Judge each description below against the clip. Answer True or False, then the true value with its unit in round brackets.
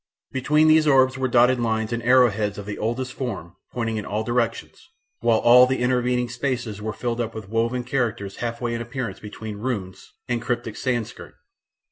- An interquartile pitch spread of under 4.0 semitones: True (2.4 semitones)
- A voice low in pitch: True (120 Hz)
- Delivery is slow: False (185 wpm)